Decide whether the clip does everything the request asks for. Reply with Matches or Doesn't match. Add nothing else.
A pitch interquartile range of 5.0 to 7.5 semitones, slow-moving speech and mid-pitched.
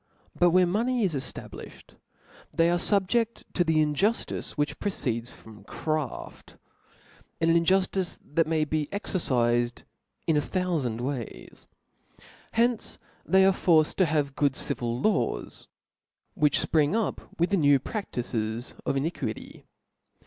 Matches